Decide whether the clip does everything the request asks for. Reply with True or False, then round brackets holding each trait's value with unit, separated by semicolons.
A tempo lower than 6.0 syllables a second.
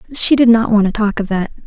False (6.4 syllables/s)